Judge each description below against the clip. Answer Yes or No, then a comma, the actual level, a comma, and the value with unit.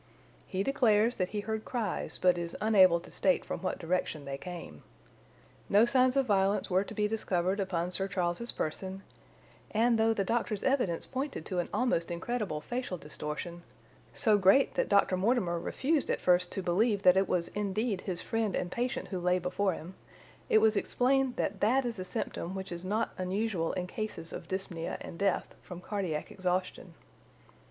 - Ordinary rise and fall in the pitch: Yes, average, 3.7 semitones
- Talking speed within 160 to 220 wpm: Yes, average, 175 wpm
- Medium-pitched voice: No, high, 195 Hz